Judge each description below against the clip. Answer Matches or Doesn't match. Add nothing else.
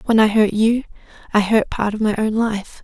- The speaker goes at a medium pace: Doesn't match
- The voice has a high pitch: Matches